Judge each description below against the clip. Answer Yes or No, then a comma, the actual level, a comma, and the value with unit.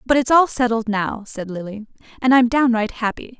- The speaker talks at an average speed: Yes, average, 195 wpm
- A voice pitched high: Yes, high, 230 Hz